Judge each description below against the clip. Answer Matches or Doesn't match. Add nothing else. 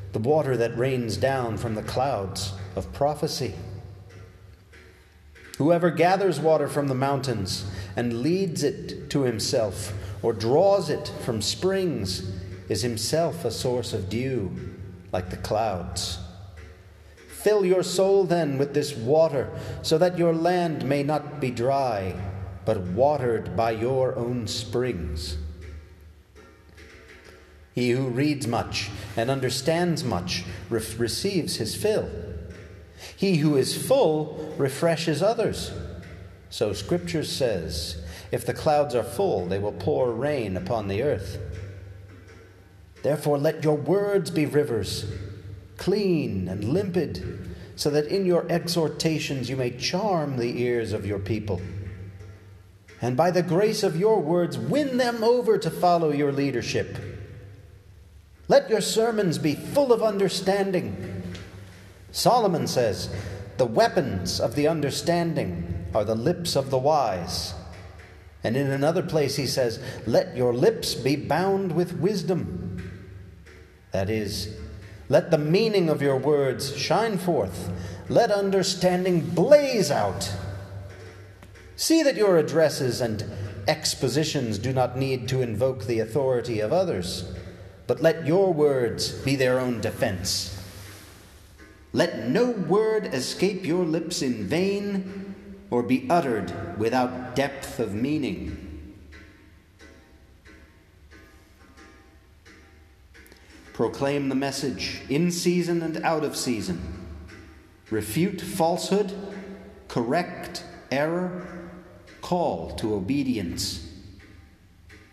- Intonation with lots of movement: Matches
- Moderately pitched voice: Doesn't match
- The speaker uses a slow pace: Matches